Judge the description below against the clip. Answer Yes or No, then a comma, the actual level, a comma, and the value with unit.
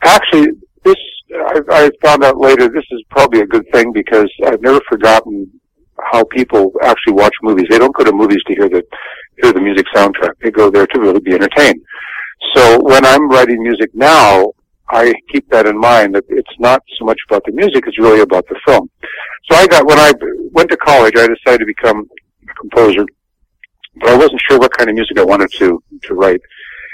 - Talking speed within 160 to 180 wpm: No, fast, 205 wpm